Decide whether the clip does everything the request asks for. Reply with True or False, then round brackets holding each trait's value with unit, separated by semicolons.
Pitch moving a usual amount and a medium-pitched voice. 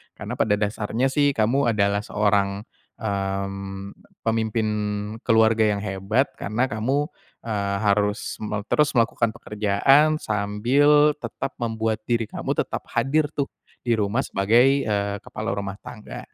False (3.2 semitones; 110 Hz)